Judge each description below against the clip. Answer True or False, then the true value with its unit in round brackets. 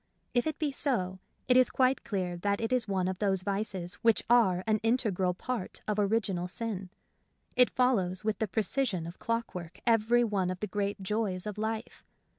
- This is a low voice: False (210 Hz)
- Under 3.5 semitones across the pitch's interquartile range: False (3.8 semitones)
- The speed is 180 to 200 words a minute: True (185 wpm)